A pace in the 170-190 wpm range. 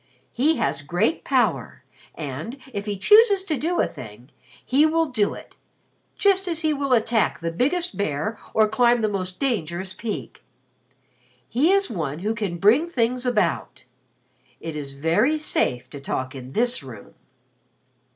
No: average, 155 wpm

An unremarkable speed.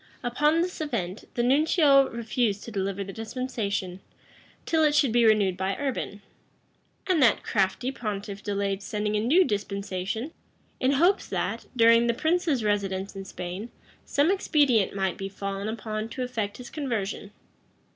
Yes: average, 150 wpm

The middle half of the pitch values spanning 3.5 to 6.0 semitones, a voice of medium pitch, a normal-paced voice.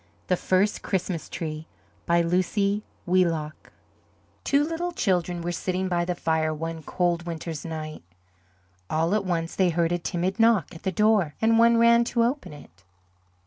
Yes: average, 4.0 semitones; medium, 175 Hz; average, 160 wpm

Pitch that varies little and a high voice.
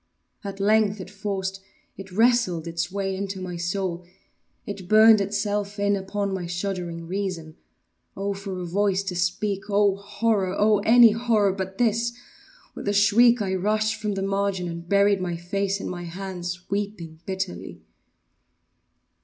Yes: narrow, 1.9 semitones; high, 195 Hz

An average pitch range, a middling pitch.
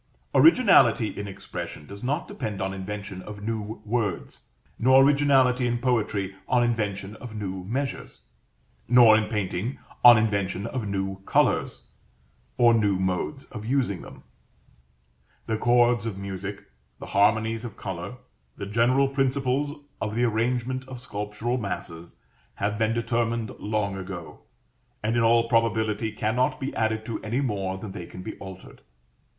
No: average, 3.4 semitones; low, 110 Hz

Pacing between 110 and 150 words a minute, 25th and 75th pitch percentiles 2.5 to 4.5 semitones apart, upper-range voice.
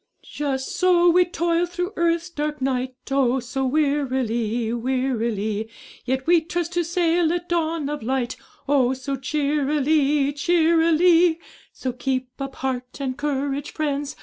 Yes: slow, 135 wpm; average, 4.2 semitones; very high, 285 Hz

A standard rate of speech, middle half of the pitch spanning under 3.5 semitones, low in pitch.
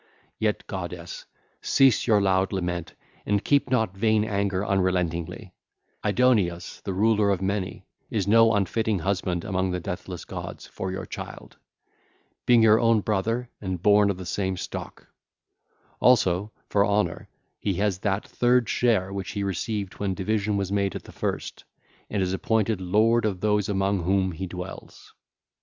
Yes: average, 155 wpm; narrow, 2.6 semitones; low, 100 Hz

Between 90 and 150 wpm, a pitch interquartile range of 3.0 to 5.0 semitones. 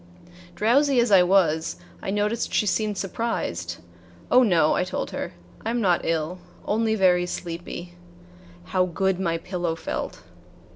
Yes: average, 145 wpm; average, 3.8 semitones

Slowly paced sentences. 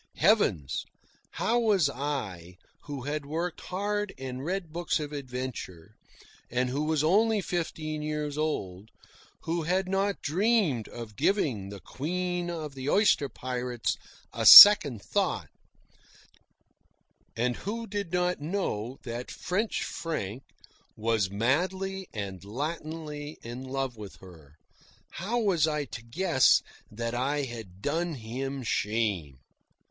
Yes: slow, 125 wpm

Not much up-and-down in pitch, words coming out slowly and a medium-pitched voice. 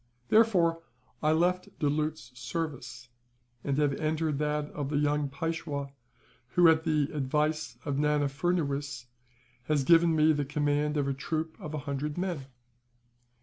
No: narrow, 2.1 semitones; average, 145 wpm; medium, 150 Hz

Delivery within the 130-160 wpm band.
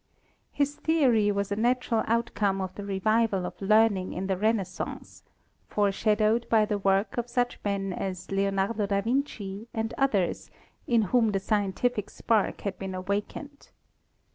Yes: average, 155 wpm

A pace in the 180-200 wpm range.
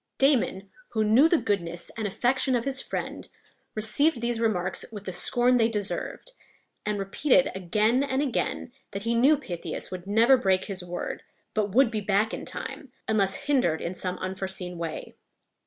No: average, 170 wpm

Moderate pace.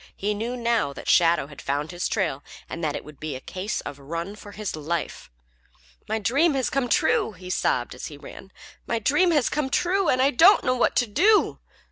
No: fast, 220 wpm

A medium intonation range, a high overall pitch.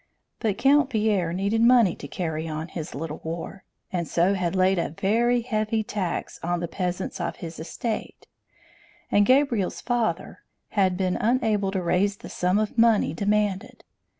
Yes: average, 4.2 semitones; high, 195 Hz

